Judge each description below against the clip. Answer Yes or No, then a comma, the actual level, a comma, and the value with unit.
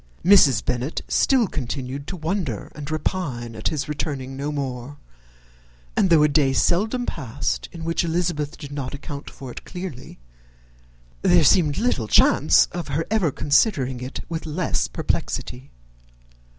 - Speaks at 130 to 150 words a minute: Yes, average, 145 wpm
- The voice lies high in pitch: No, medium, 150 Hz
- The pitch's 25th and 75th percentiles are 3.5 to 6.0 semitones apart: Yes, average, 4.4 semitones